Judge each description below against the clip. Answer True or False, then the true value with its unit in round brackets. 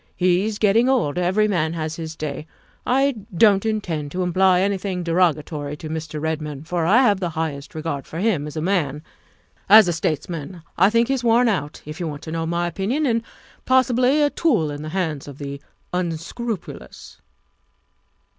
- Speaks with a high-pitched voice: False (175 Hz)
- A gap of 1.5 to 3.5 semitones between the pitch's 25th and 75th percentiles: False (5.5 semitones)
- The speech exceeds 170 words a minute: True (185 wpm)